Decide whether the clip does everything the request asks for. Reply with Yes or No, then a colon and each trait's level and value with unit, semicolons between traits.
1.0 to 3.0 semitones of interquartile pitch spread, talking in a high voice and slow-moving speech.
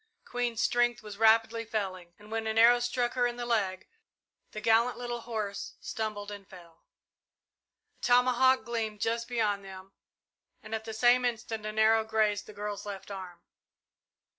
No: narrow, 2.6 semitones; high, 220 Hz; average, 165 wpm